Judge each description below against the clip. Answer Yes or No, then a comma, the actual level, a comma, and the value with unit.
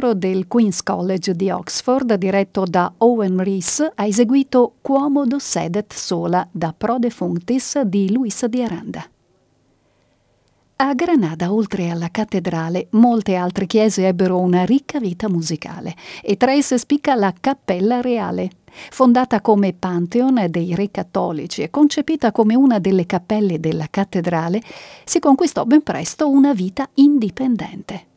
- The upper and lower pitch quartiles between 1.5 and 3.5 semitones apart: No, wide, 5.4 semitones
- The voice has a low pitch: No, high, 210 Hz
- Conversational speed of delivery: Yes, average, 135 wpm